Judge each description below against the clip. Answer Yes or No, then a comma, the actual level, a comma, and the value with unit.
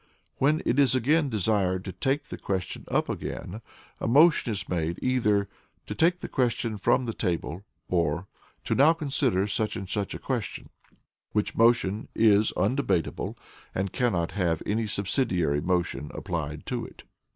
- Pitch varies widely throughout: Yes, wide, 5.7 semitones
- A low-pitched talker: Yes, low, 105 Hz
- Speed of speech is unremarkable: Yes, average, 150 wpm